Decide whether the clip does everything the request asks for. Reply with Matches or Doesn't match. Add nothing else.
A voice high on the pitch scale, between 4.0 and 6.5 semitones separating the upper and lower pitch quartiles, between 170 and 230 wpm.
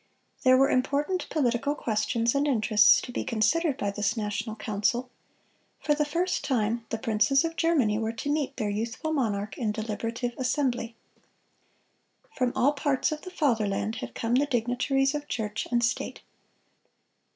Doesn't match